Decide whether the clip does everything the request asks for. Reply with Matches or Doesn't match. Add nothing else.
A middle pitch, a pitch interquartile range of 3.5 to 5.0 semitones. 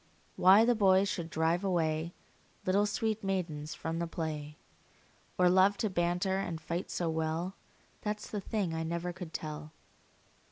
Doesn't match